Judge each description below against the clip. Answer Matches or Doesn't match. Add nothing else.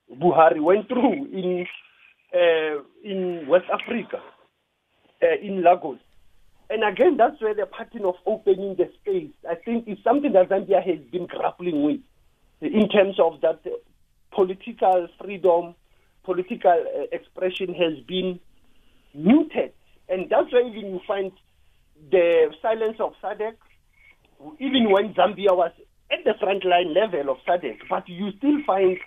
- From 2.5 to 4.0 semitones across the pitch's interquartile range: Doesn't match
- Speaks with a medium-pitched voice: Doesn't match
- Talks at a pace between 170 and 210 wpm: Doesn't match